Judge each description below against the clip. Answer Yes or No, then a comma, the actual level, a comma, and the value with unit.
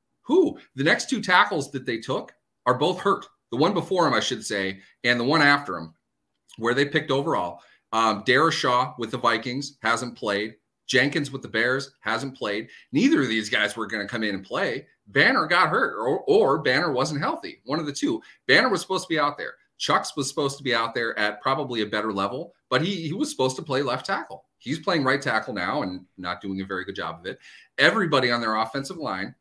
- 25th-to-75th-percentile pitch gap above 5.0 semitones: Yes, wide, 5.4 semitones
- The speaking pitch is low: Yes, low, 125 Hz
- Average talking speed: No, fast, 225 wpm